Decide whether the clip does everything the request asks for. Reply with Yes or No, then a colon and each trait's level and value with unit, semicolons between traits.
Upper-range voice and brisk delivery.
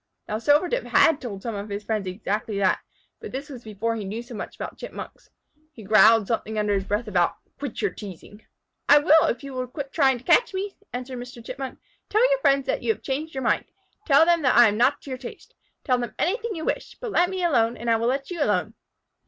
Yes: high, 245 Hz; fast, 235 wpm